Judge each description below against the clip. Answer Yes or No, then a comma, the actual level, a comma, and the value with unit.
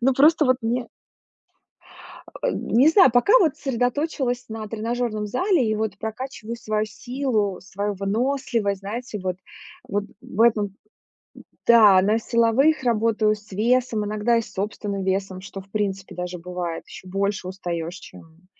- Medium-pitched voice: No, high, 215 Hz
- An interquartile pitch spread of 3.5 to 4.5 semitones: Yes, average, 3.8 semitones